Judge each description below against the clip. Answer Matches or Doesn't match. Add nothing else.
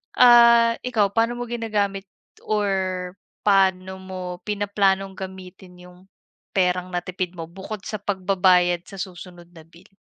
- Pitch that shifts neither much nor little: Doesn't match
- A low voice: Doesn't match